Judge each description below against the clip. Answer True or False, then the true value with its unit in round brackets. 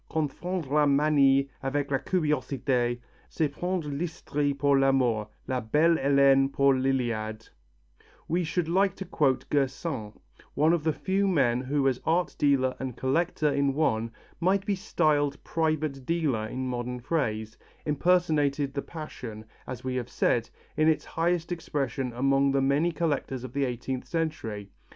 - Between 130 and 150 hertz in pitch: True (140 Hz)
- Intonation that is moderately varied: True (3.5 semitones)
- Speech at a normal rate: True (150 wpm)